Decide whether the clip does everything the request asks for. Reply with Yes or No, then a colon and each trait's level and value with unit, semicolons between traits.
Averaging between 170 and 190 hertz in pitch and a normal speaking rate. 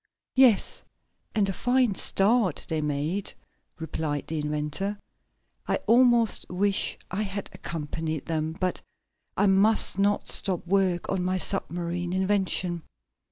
No: medium, 185 Hz; slow, 120 wpm